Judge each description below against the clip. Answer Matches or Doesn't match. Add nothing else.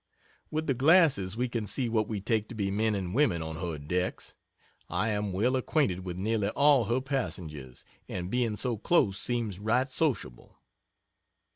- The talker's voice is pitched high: Doesn't match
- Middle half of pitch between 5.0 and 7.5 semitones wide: Matches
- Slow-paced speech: Doesn't match